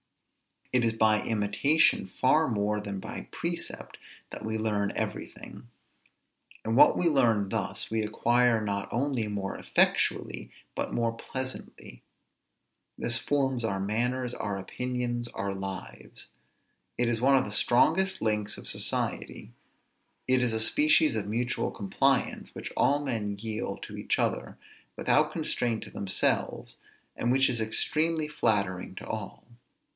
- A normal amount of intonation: Yes, average, 3.7 semitones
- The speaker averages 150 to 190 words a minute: No, average, 140 wpm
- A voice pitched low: Yes, low, 115 Hz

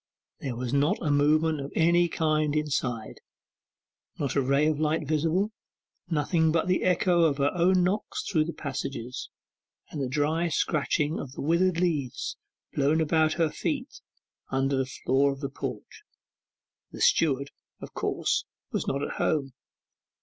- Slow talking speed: No, average, 155 wpm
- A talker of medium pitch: Yes, medium, 150 Hz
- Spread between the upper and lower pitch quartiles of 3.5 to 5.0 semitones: No, average, 3.0 semitones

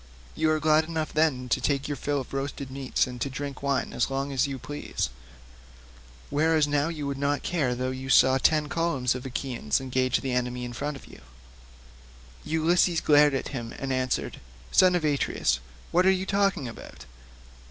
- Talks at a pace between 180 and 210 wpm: Yes, average, 185 wpm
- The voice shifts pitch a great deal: No, average, 3.2 semitones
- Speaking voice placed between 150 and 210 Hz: No, medium, 140 Hz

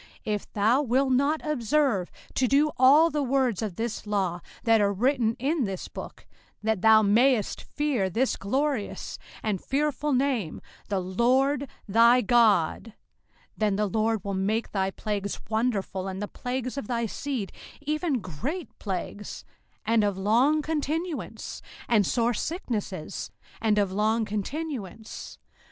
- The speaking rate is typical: Yes, average, 145 wpm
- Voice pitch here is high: Yes, high, 230 Hz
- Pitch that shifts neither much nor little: Yes, average, 5.0 semitones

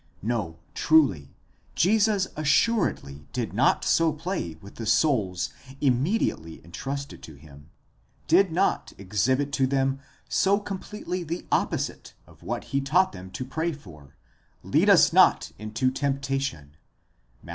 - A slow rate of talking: Yes, slow, 130 wpm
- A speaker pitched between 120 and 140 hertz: Yes, low, 135 Hz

